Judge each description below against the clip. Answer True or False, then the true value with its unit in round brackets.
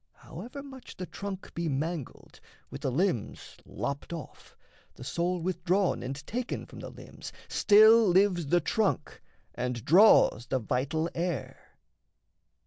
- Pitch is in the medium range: True (175 Hz)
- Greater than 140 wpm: False (135 wpm)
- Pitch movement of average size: False (6.2 semitones)